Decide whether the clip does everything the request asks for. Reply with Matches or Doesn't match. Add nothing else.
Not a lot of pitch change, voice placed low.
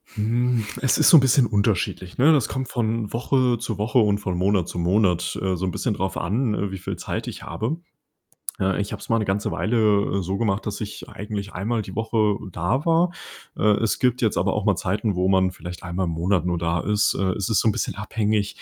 Doesn't match